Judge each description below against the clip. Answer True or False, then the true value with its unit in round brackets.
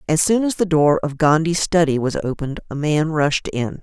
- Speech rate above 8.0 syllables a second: False (5.2 syllables/s)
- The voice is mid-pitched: True (155 Hz)